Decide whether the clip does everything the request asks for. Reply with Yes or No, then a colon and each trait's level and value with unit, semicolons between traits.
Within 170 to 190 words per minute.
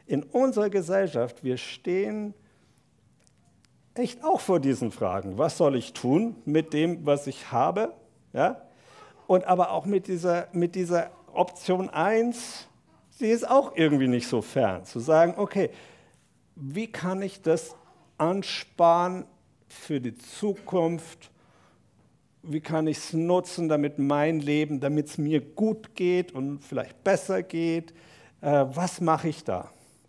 No: average, 135 wpm